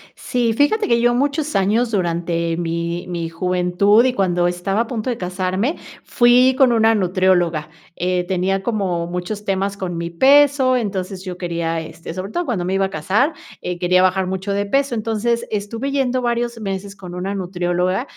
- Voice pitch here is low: No, high, 195 Hz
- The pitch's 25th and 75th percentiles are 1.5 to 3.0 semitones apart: No, average, 4.9 semitones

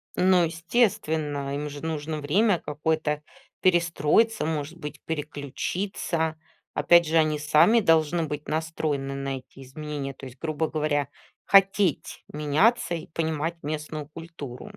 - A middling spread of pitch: No, narrow, 2.3 semitones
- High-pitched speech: No, medium, 155 Hz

